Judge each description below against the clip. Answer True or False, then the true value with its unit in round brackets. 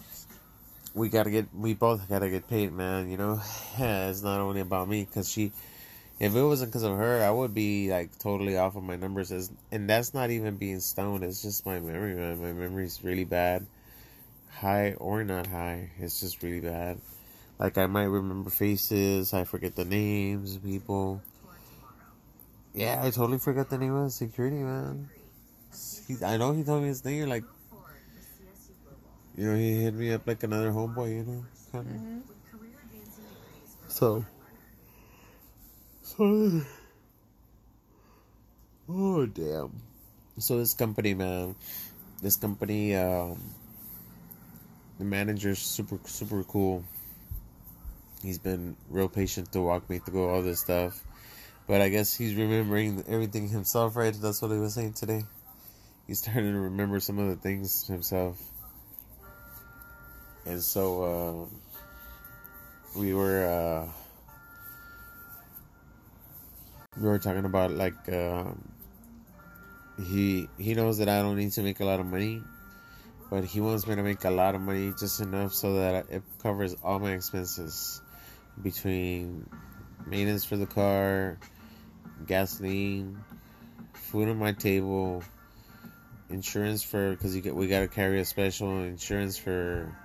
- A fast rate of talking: False (140 wpm)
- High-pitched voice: False (100 Hz)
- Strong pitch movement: False (2.9 semitones)